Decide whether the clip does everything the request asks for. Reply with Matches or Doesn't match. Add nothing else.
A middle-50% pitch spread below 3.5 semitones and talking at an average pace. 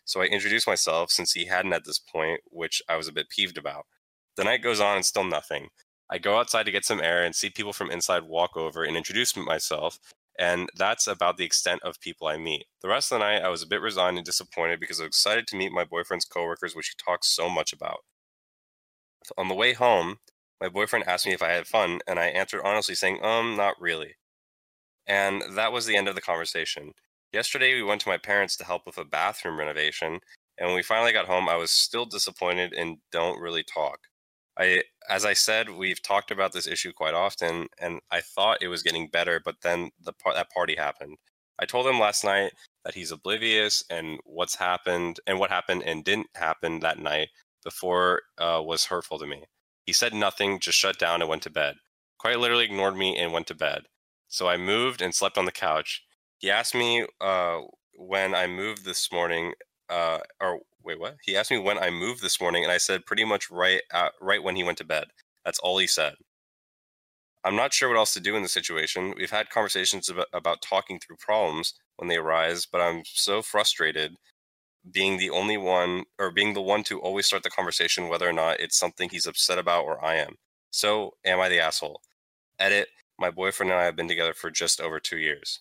Doesn't match